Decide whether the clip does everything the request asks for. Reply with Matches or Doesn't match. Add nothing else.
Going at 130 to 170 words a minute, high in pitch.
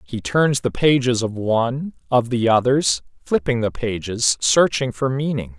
Doesn't match